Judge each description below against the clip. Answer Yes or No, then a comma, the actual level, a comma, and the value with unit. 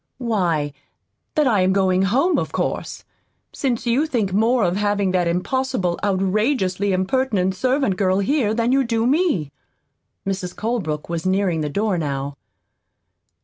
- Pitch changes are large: No, average, 4.8 semitones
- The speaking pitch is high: Yes, high, 200 Hz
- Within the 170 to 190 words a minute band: No, average, 145 wpm